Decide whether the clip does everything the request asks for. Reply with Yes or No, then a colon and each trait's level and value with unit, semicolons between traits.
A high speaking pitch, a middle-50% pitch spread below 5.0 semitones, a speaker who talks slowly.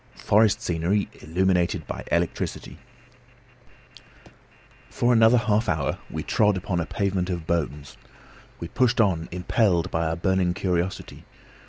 No: very low, 90 Hz; average, 3.4 semitones; slow, 125 wpm